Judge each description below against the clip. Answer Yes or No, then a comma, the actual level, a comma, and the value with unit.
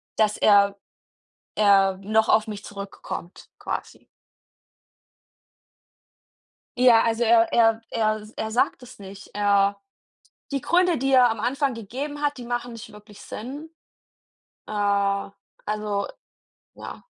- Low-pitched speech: No, high, 215 Hz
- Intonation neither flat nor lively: Yes, average, 3.2 semitones